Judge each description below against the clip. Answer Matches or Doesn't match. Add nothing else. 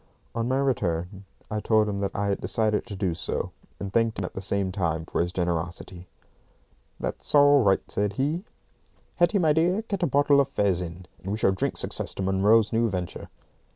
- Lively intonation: Matches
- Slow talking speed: Doesn't match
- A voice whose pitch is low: Matches